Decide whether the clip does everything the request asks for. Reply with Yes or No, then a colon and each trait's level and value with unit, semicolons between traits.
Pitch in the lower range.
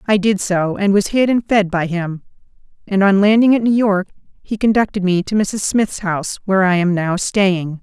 No: high, 195 Hz